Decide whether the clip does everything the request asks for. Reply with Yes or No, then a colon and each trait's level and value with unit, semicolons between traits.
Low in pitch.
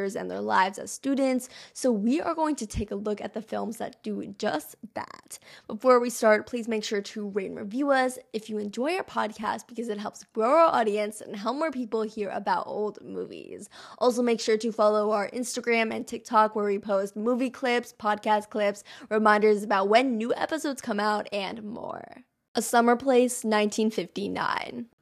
No: high, 225 Hz